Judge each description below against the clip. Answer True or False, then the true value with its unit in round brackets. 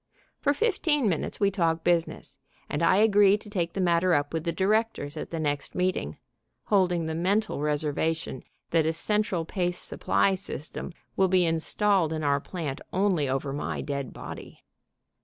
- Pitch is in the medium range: True (170 Hz)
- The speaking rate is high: False (165 wpm)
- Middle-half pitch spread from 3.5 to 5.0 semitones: True (4.0 semitones)